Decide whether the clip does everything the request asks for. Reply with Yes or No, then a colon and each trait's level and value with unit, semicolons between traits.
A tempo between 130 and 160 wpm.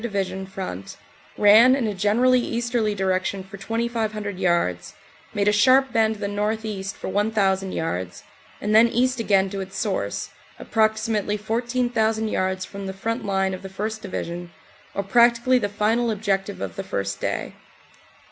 Yes: average, 155 wpm